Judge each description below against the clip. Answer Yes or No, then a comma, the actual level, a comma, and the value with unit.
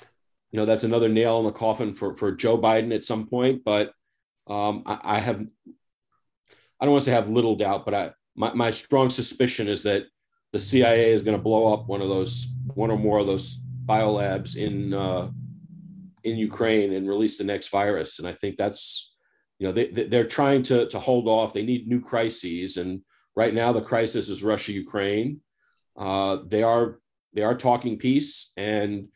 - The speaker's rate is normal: Yes, average, 195 wpm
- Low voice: Yes, low, 110 Hz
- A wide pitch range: No, average, 2.9 semitones